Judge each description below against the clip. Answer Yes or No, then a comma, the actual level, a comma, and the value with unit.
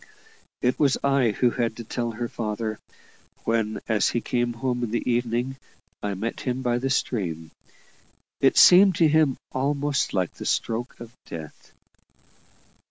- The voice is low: Yes, low, 120 Hz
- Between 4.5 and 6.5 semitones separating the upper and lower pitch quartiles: No, average, 2.9 semitones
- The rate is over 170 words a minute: No, average, 155 wpm